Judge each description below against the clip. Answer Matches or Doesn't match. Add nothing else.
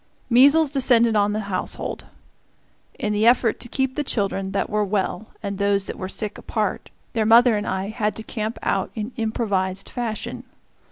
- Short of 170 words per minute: Doesn't match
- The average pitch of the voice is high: Matches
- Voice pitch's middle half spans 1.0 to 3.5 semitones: Matches